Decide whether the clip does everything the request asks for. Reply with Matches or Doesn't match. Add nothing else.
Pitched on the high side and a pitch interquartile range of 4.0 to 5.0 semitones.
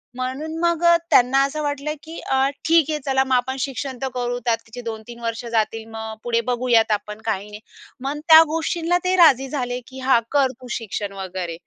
Matches